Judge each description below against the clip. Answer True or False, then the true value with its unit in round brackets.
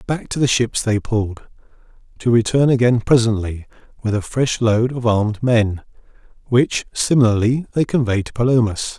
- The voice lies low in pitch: True (115 Hz)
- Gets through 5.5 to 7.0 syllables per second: False (5.0 syllables/s)